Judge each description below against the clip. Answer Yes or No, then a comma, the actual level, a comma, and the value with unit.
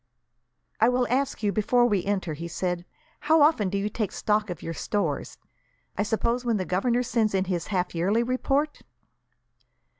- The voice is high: Yes, high, 210 Hz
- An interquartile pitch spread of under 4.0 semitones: No, average, 4.6 semitones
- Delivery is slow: No, average, 175 wpm